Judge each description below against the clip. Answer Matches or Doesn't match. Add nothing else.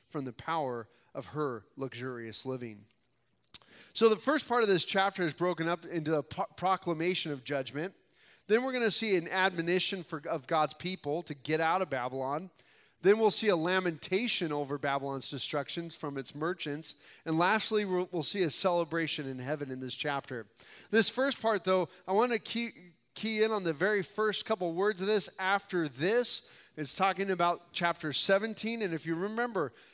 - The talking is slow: Doesn't match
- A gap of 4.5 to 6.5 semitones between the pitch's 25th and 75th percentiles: Matches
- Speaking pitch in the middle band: Matches